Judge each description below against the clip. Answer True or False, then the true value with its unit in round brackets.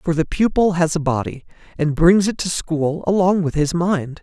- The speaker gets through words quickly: True (215 wpm)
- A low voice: False (170 Hz)